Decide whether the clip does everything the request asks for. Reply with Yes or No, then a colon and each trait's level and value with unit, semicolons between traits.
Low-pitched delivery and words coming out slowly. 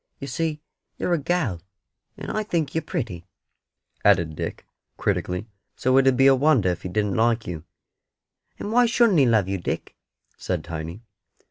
No: low, 120 Hz; average, 170 wpm